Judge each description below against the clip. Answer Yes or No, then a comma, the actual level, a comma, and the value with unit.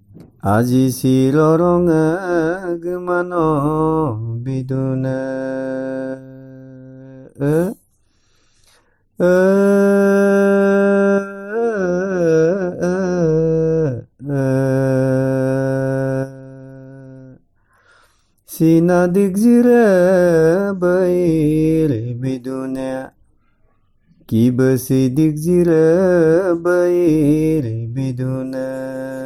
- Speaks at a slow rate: Yes, slow, 40 wpm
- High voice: No, medium, 155 Hz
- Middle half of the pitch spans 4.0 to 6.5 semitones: Yes, average, 5.1 semitones